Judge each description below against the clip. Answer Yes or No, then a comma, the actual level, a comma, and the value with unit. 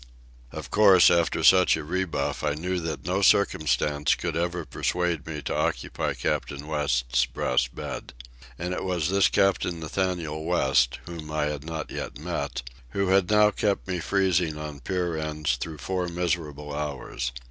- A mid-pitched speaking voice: No, very low, 80 Hz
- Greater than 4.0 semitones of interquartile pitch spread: No, average, 3.5 semitones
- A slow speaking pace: No, average, 160 wpm